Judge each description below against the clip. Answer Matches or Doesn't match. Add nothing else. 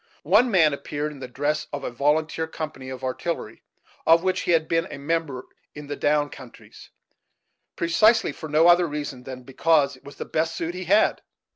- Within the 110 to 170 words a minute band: Doesn't match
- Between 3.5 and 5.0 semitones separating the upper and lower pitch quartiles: Doesn't match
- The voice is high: Doesn't match